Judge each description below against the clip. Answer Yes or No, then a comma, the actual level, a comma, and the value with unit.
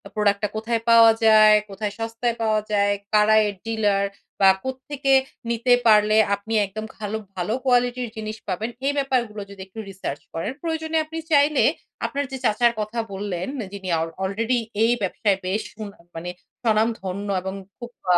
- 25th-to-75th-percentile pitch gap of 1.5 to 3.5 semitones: Yes, average, 3.0 semitones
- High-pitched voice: Yes, high, 215 Hz